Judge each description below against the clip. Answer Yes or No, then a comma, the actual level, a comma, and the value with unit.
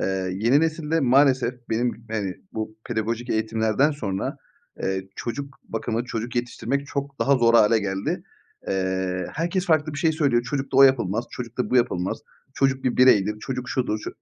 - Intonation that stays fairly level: No, average, 4.0 semitones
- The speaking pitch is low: Yes, low, 120 Hz